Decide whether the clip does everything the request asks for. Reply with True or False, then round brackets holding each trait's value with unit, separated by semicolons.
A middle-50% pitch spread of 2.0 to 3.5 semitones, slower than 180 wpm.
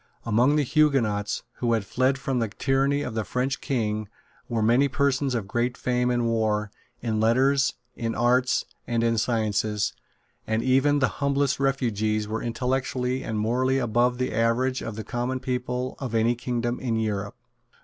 True (2.8 semitones; 165 wpm)